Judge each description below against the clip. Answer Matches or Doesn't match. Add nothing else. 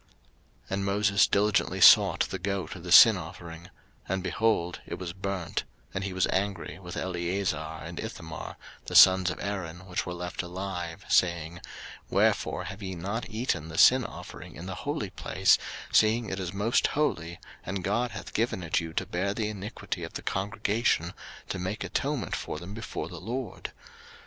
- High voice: Doesn't match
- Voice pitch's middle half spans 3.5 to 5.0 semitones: Doesn't match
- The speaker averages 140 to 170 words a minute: Doesn't match